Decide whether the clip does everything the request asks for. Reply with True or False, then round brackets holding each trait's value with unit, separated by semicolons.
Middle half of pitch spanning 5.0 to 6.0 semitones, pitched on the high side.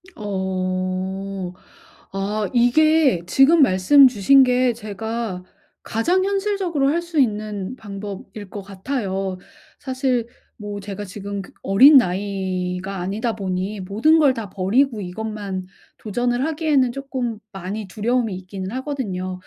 True (5.3 semitones; 210 Hz)